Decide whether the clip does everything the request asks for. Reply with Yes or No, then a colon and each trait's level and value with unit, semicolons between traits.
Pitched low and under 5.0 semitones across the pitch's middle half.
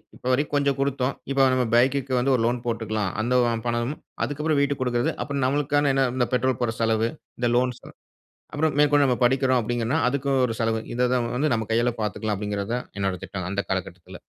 Yes: low, 125 Hz; average, 3.5 semitones